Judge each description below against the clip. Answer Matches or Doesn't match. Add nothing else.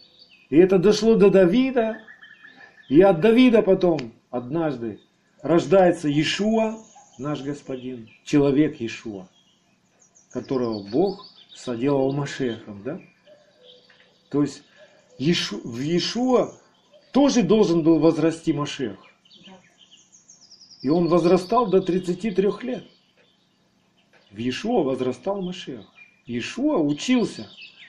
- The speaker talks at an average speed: Doesn't match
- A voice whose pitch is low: Doesn't match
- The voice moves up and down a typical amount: Doesn't match